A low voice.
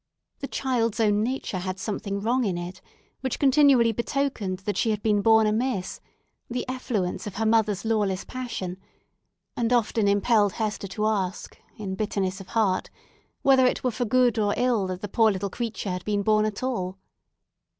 No: high, 215 Hz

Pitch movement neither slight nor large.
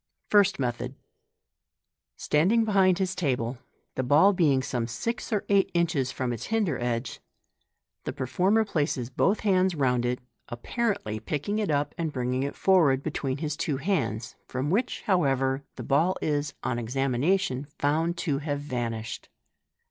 No: wide, 6.5 semitones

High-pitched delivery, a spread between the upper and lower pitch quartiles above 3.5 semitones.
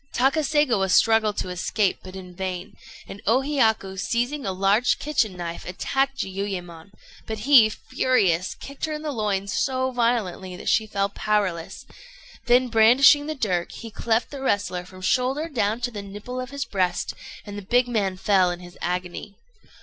Yes: high, 210 Hz; average, 5.1 semitones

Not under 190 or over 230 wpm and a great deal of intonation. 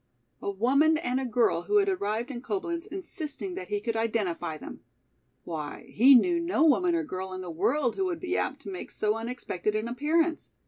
Yes: average, 200 wpm; wide, 7.9 semitones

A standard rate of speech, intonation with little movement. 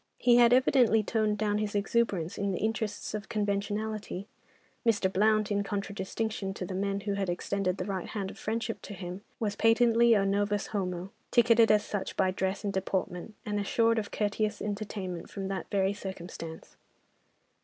Yes: average, 165 wpm; narrow, 2.1 semitones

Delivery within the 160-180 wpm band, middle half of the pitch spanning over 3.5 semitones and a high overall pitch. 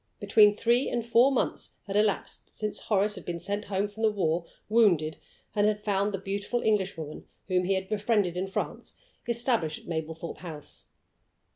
No: average, 170 wpm; average, 3.0 semitones; high, 200 Hz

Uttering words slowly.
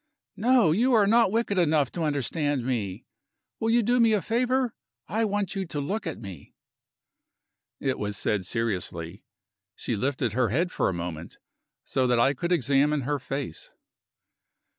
No: average, 160 wpm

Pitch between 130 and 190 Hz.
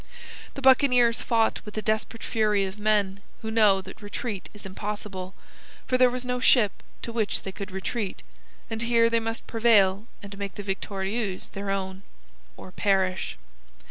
No: high, 210 Hz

